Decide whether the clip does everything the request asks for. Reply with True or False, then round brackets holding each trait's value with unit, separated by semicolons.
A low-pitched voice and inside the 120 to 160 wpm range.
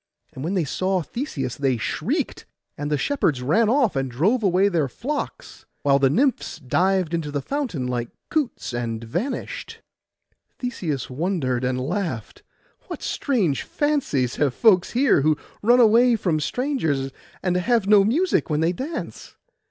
False (175 Hz; 150 wpm)